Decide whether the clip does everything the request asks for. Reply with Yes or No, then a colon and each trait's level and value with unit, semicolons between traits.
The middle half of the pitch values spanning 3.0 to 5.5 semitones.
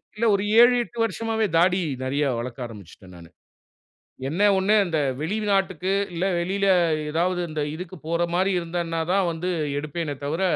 Yes: average, 4.0 semitones